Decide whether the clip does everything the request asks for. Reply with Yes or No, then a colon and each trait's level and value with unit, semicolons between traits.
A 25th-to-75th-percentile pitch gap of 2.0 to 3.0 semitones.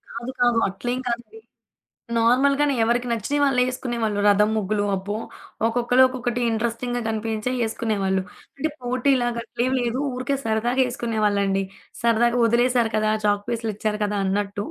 Yes: narrow, 2.6 semitones